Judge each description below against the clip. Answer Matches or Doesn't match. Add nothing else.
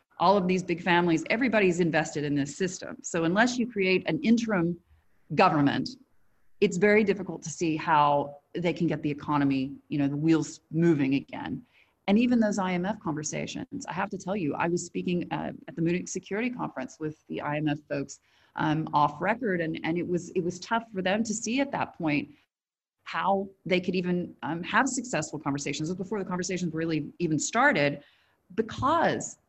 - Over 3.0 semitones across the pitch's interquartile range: Matches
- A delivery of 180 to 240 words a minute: Matches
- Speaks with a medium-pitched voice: Matches